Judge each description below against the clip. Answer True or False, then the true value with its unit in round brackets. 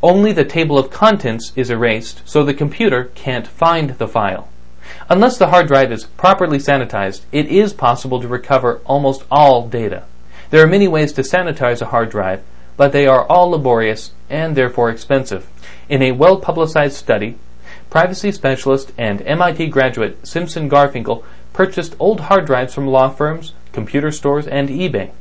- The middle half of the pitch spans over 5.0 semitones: True (5.4 semitones)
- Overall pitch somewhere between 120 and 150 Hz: True (135 Hz)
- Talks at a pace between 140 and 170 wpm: True (160 wpm)